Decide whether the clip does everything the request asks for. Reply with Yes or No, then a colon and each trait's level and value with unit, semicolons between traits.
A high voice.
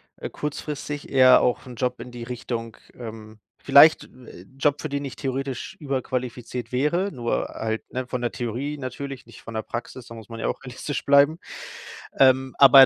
No: low, 130 Hz